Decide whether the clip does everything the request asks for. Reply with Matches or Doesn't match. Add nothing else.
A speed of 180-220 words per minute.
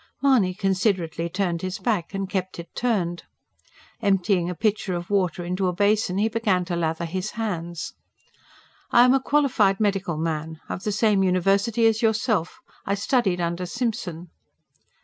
Doesn't match